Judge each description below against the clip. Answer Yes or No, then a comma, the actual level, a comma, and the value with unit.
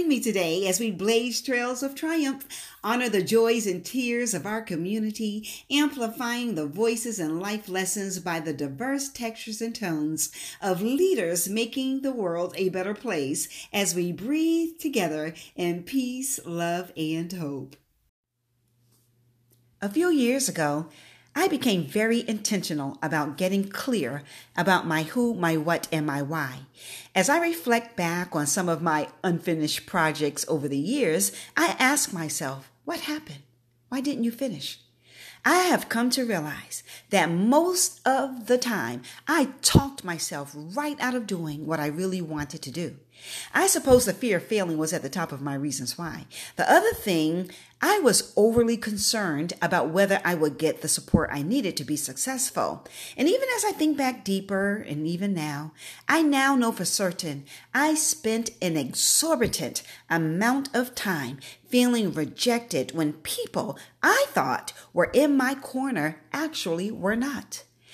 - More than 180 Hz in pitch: Yes, high, 190 Hz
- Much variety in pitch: Yes, wide, 7.9 semitones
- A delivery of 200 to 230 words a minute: No, average, 155 wpm